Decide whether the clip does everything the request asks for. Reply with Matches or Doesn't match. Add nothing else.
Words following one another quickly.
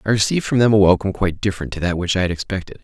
Matches